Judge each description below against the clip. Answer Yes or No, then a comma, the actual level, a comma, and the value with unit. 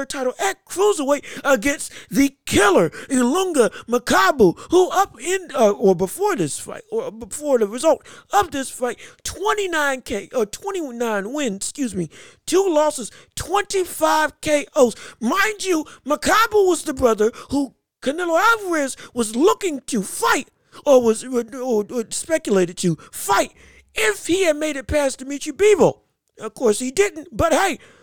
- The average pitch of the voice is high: Yes, very high, 290 Hz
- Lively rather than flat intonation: Yes, wide, 7.1 semitones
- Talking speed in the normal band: Yes, average, 145 wpm